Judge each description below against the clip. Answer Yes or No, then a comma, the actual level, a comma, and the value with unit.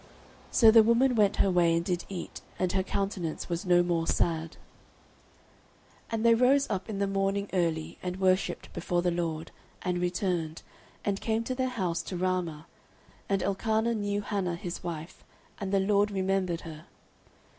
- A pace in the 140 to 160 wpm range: No, average, 170 wpm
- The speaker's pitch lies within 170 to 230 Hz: Yes, medium, 185 Hz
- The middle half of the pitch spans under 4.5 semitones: Yes, average, 2.9 semitones